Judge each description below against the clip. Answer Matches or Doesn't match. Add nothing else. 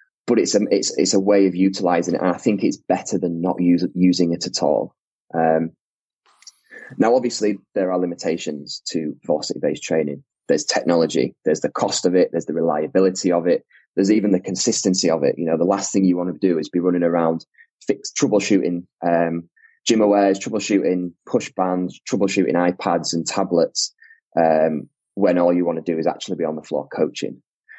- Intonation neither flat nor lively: Doesn't match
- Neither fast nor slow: Matches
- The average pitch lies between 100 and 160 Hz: Doesn't match